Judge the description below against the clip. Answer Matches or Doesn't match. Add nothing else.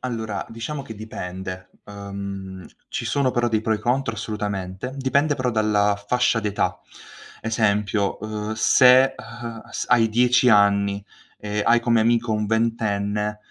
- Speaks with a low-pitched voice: Matches